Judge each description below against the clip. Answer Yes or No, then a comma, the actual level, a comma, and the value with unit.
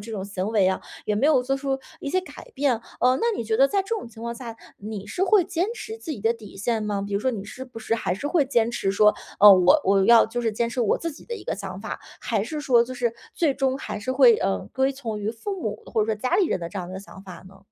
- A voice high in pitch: Yes, high, 230 Hz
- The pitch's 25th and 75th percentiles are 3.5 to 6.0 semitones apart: Yes, average, 4.7 semitones